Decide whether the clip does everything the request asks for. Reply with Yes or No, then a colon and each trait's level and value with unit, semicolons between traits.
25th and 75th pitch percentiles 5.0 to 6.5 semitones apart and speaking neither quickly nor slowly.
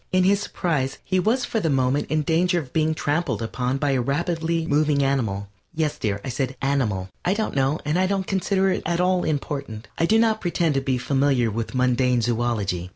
No: wide, 5.5 semitones; fast, 210 wpm